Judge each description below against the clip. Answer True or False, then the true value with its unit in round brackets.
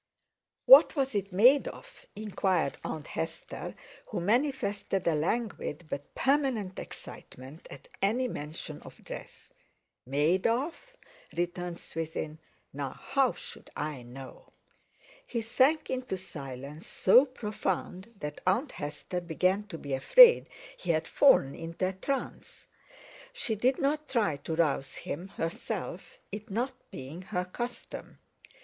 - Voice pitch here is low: False (185 Hz)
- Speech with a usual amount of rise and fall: False (7.5 semitones)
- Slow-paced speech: True (130 wpm)